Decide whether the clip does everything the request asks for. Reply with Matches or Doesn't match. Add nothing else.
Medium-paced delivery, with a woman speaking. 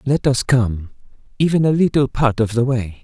Doesn't match